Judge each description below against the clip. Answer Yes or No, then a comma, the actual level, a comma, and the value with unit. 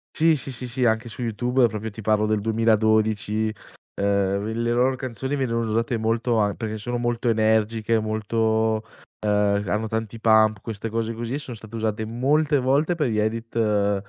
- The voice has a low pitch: Yes, low, 110 Hz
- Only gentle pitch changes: Yes, narrow, 1.7 semitones